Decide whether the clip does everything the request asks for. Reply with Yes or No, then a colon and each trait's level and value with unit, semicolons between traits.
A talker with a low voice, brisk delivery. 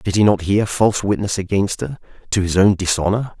Yes: low, 100 Hz; fast, 210 wpm